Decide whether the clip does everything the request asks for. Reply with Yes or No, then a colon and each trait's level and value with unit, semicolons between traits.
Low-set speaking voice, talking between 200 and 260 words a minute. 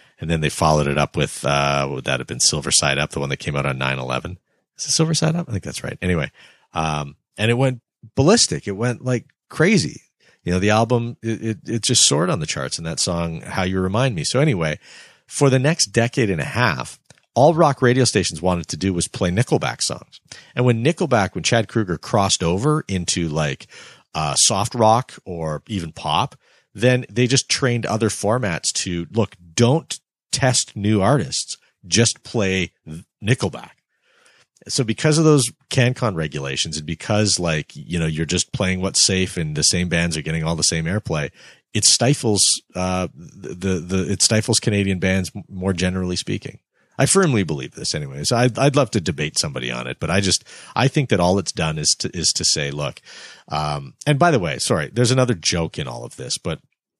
Yes: low, 100 Hz; fast, 205 wpm